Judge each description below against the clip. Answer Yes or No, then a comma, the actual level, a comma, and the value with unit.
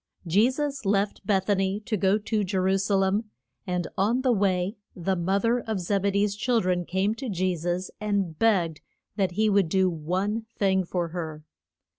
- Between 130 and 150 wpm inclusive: No, average, 200 wpm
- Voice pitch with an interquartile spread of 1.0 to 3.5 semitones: Yes, narrow, 2.6 semitones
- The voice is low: No, high, 195 Hz